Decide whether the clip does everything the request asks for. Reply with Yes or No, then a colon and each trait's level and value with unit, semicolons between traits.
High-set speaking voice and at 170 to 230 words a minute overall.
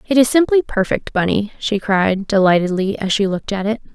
Yes: high, 210 Hz; average, 200 wpm